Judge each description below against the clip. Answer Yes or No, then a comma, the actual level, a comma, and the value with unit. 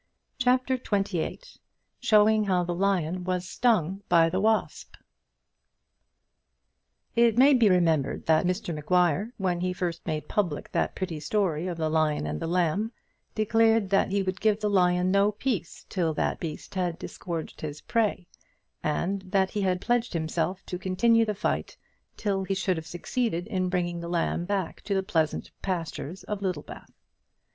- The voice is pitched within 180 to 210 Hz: Yes, medium, 185 Hz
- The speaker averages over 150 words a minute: Yes, average, 160 wpm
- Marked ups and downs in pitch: No, average, 3.5 semitones